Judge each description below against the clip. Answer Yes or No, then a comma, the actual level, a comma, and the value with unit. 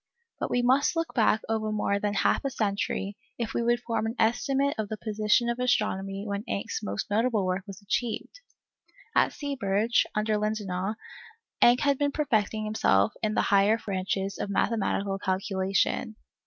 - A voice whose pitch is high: Yes, high, 215 Hz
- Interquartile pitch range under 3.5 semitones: Yes, average, 3.1 semitones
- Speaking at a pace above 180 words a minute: No, average, 165 wpm